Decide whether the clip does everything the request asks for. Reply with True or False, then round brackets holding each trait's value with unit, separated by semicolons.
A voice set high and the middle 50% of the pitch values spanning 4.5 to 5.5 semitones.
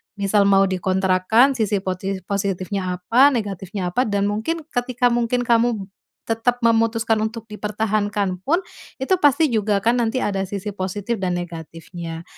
False (205 Hz; 3.5 semitones)